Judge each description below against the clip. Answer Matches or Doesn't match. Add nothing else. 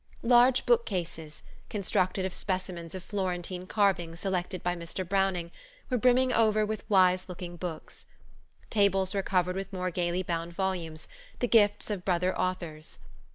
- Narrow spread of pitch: Matches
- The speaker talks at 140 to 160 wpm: Matches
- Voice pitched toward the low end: Doesn't match